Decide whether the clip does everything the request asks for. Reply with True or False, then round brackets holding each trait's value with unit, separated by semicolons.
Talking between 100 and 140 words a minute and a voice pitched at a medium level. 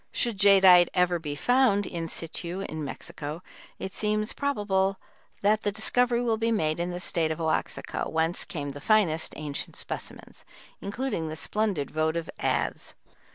False (155 wpm; 180 Hz)